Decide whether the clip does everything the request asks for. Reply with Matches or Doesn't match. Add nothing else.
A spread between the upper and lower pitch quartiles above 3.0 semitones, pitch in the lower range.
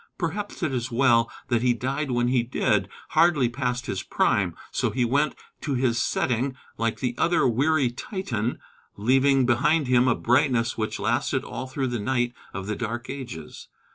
Doesn't match